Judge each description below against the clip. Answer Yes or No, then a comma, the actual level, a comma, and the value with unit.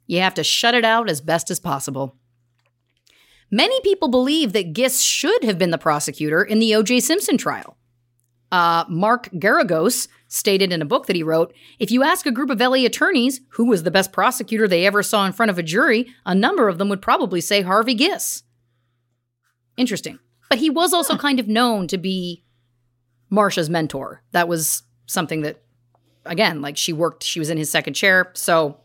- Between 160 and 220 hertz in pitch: Yes, medium, 185 Hz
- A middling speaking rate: Yes, average, 190 wpm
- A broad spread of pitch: Yes, wide, 7.8 semitones